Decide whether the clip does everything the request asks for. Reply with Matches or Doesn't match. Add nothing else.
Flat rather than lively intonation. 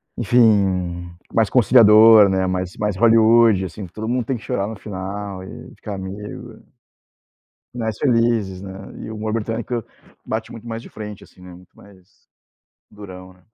Doesn't match